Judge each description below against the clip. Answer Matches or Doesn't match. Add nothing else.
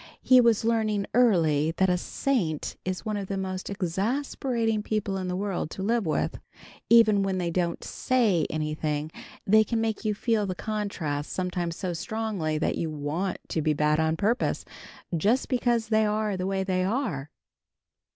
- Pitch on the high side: Matches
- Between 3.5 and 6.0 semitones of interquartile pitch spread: Matches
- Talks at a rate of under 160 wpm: Doesn't match